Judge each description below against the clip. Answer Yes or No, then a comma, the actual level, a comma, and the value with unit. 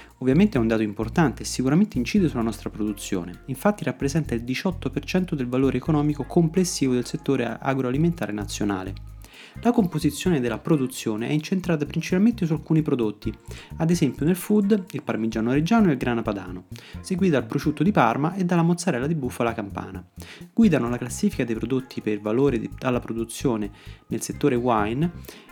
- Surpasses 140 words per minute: Yes, average, 160 wpm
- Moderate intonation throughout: No, wide, 6.8 semitones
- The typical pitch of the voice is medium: No, low, 130 Hz